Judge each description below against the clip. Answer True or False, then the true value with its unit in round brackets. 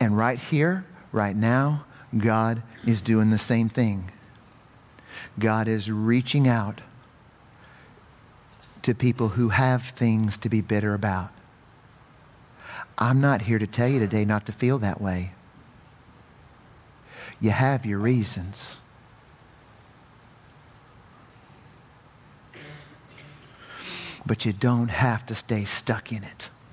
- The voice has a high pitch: False (115 Hz)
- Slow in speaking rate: True (110 wpm)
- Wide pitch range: False (2.8 semitones)